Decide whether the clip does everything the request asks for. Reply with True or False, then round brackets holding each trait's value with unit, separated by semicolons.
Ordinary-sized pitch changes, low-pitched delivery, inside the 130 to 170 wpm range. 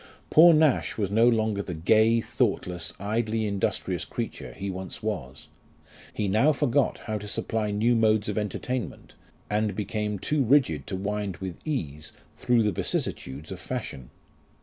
True (3.3 semitones; 105 Hz; 150 wpm)